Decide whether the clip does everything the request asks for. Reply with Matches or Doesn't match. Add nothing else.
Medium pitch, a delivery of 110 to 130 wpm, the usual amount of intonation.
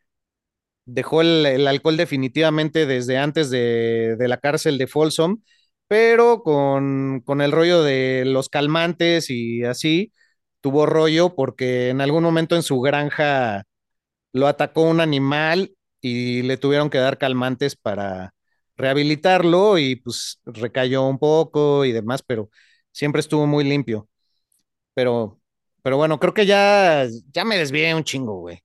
Doesn't match